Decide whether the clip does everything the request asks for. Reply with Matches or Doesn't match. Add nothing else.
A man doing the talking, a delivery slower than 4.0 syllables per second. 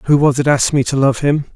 Doesn't match